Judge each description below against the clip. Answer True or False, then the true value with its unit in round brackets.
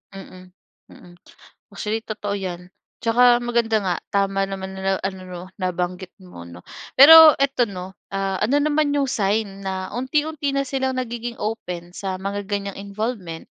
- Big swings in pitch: False (4.4 semitones)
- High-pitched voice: True (200 Hz)